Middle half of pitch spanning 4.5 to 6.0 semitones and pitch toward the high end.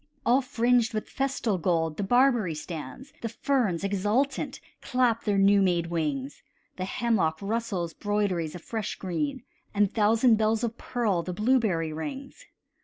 Yes: wide, 5.4 semitones; high, 210 Hz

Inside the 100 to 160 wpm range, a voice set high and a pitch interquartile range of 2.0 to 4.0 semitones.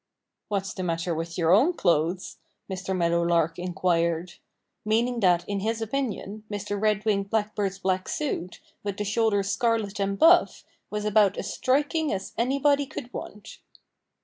Yes: average, 150 wpm; high, 200 Hz; average, 3.5 semitones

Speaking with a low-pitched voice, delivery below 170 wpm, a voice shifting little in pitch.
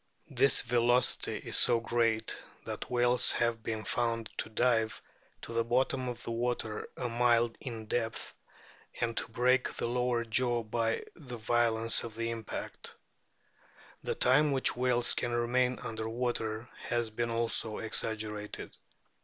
Yes: low, 120 Hz; average, 140 wpm; narrow, 1.5 semitones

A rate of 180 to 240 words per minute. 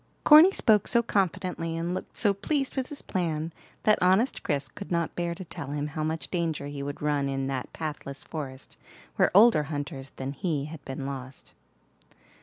Yes: average, 185 wpm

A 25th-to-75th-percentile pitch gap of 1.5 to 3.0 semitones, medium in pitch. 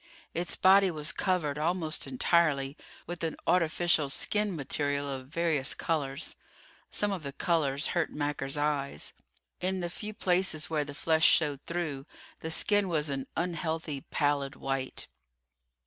No: average, 3.5 semitones; medium, 155 Hz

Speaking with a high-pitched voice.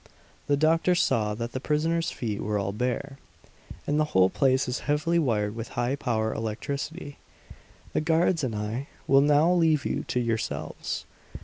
No: low, 135 Hz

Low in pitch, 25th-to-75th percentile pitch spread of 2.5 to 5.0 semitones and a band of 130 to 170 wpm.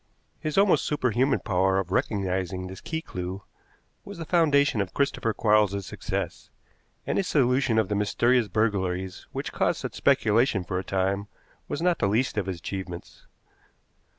No: low, 105 Hz; wide, 5.5 semitones; average, 155 wpm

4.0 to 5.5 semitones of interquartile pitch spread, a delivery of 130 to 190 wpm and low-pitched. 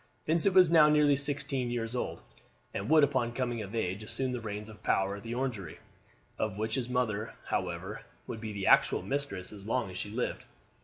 No: average, 4.4 semitones; average, 200 wpm; low, 115 Hz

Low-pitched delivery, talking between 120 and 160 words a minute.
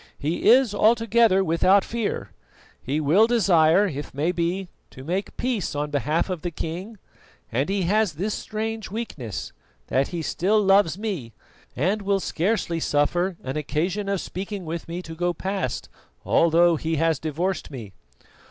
No: medium, 175 Hz; average, 155 wpm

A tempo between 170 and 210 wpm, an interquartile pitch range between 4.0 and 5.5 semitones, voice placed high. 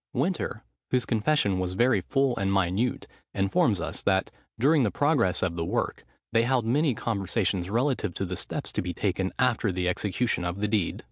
No: average, 185 wpm; average, 5.2 semitones; low, 105 Hz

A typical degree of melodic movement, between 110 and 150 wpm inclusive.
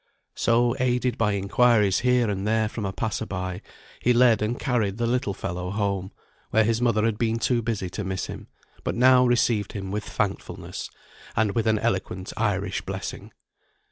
No: average, 3.2 semitones; average, 175 wpm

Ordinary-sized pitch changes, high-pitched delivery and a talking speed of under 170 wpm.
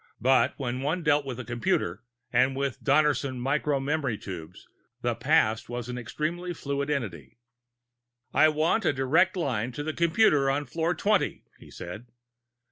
No: average, 4.0 semitones; medium, 140 Hz; average, 155 wpm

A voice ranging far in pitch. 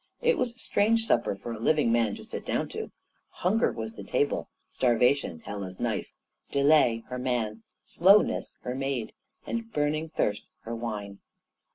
Yes: wide, 5.9 semitones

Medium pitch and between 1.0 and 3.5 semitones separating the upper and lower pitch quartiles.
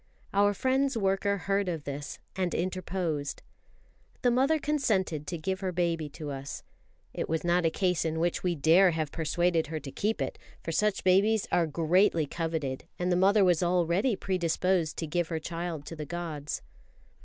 Yes: medium, 175 Hz; average, 3.2 semitones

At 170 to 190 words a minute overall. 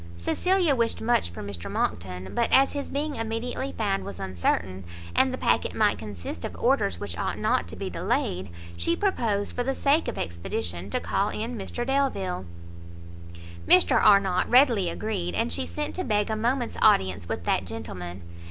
Yes: average, 175 wpm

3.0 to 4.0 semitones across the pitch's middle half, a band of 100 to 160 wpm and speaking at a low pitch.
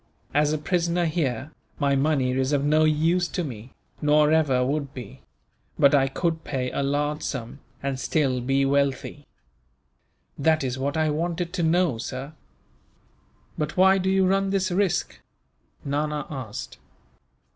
No: average, 3.4 semitones; average, 150 wpm; medium, 150 Hz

